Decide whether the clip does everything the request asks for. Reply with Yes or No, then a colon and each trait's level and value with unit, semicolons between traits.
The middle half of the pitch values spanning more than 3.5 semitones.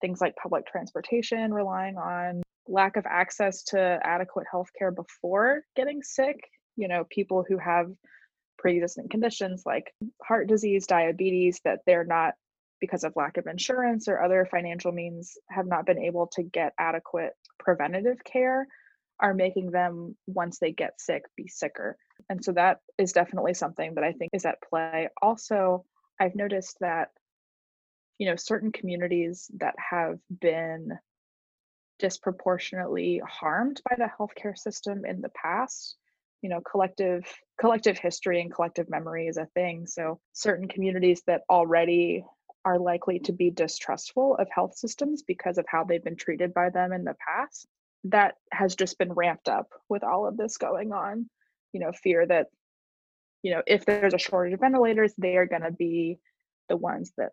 No: average, 3.2 semitones